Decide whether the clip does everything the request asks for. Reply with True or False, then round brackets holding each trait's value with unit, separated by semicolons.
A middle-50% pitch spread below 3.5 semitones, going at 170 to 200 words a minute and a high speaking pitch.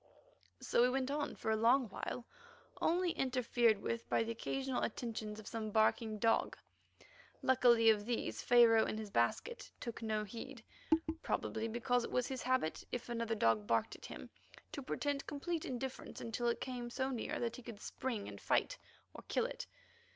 True (2.9 semitones; 175 wpm; 235 Hz)